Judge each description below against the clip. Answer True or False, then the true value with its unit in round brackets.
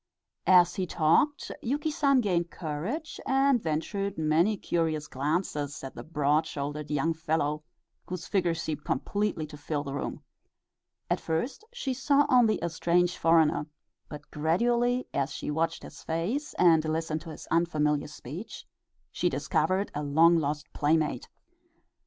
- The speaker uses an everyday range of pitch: True (4.9 semitones)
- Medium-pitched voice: True (165 Hz)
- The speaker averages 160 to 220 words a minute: False (145 wpm)